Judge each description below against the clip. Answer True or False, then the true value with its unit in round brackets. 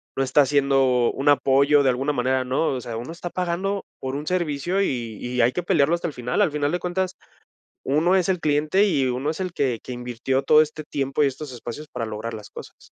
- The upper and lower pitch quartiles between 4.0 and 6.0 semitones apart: True (4.4 semitones)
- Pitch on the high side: False (140 Hz)